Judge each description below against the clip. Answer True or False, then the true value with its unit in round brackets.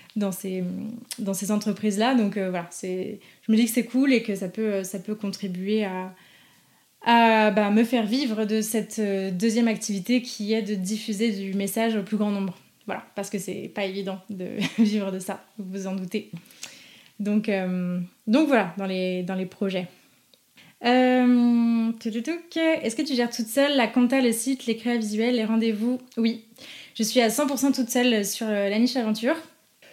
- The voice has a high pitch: True (220 Hz)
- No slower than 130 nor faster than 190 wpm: True (185 wpm)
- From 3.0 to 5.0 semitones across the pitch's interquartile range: True (3.3 semitones)